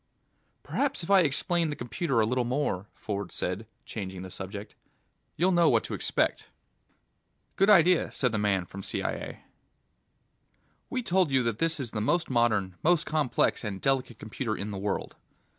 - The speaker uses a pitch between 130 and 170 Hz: No, low, 120 Hz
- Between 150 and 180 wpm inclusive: Yes, average, 165 wpm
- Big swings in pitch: Yes, wide, 8.1 semitones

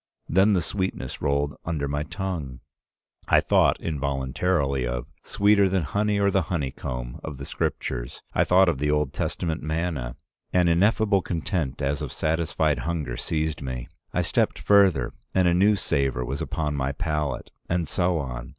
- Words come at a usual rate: Yes, average, 160 wpm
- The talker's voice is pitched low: Yes, very low, 80 Hz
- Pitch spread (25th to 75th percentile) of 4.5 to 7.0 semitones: Yes, average, 5.0 semitones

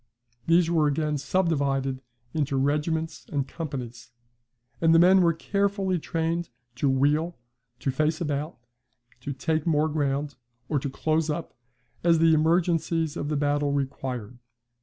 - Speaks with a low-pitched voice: No, medium, 155 Hz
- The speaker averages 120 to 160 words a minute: Yes, average, 140 wpm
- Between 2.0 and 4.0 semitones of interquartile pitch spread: Yes, average, 2.8 semitones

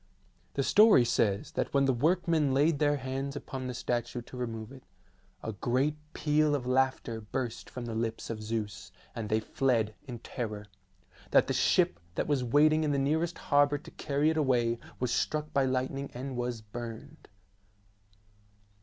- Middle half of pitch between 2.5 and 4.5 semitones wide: Yes, average, 3.7 semitones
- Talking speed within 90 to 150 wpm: No, average, 170 wpm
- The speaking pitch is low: Yes, low, 130 Hz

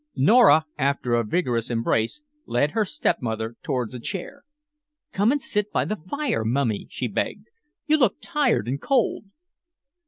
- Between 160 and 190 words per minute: No, average, 150 wpm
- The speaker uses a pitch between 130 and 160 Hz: Yes, medium, 140 Hz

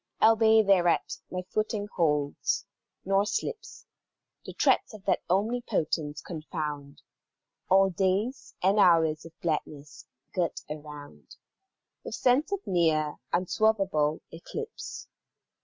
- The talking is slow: Yes, slow, 105 wpm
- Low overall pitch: No, medium, 180 Hz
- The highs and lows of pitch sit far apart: Yes, wide, 5.7 semitones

